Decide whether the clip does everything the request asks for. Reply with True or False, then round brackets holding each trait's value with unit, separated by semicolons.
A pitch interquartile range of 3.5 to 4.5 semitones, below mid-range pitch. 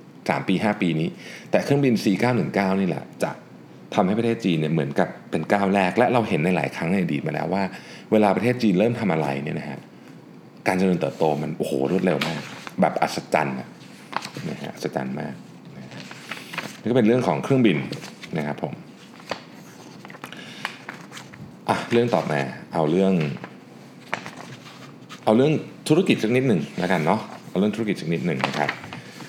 False (5.1 semitones; 95 Hz)